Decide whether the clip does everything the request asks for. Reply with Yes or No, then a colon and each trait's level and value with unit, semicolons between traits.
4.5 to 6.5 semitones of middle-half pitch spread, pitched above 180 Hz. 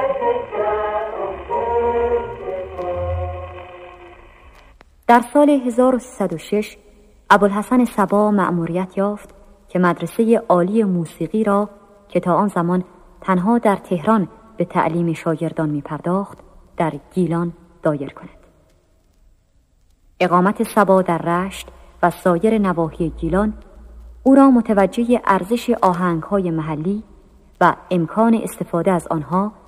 No: average, 4.0 semitones; high, 190 Hz